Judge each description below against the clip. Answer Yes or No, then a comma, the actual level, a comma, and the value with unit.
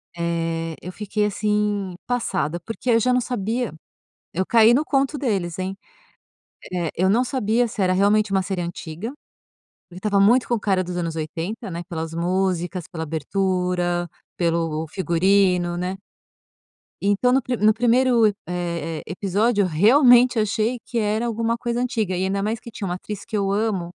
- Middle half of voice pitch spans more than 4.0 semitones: Yes, average, 4.4 semitones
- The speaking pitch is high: Yes, high, 195 Hz